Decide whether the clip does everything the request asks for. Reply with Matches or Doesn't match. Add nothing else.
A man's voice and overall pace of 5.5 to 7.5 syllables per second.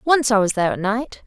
Doesn't match